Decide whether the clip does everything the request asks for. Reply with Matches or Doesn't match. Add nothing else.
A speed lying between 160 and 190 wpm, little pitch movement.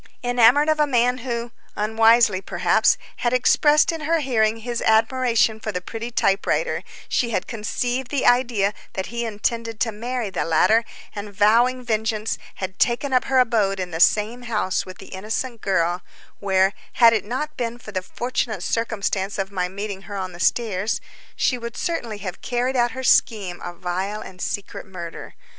Doesn't match